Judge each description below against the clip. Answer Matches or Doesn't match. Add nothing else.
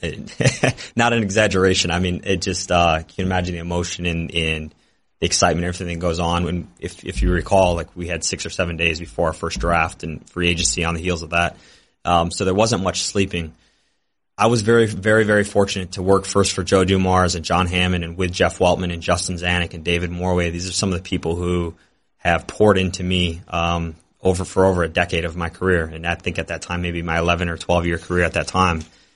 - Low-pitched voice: Matches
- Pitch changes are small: Matches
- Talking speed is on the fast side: Matches